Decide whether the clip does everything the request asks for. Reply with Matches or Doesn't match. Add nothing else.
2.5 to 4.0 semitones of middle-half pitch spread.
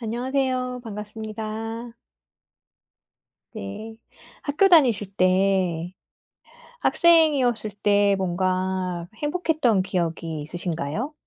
Doesn't match